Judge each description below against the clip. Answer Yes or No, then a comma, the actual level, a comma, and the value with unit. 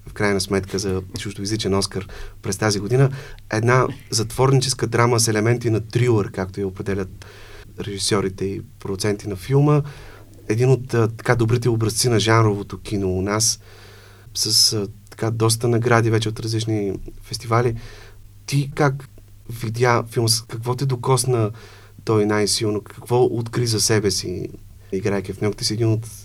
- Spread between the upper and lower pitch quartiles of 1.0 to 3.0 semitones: Yes, average, 2.7 semitones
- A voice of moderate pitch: No, low, 110 Hz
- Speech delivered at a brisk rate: No, average, 140 wpm